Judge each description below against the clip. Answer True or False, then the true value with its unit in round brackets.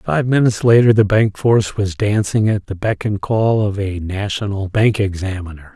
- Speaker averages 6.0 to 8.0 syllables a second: False (4.9 syllables/s)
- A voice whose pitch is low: True (105 Hz)